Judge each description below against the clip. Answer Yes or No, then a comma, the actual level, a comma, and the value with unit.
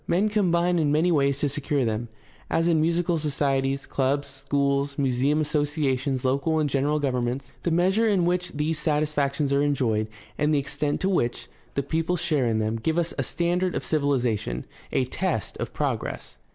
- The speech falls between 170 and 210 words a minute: Yes, average, 180 wpm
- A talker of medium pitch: Yes, medium, 145 Hz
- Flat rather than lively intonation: No, average, 3.3 semitones